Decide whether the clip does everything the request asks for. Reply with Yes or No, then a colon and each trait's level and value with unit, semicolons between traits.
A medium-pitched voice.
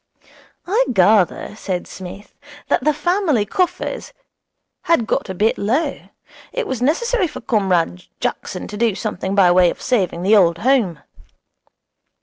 No: high, 215 Hz